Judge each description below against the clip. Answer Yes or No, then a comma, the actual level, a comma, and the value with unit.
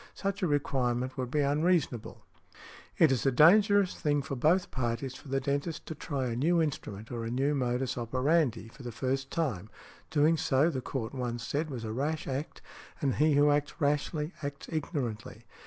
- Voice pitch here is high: No, medium, 140 Hz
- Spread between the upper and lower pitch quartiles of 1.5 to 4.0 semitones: Yes, average, 3.6 semitones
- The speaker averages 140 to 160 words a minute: No, average, 180 wpm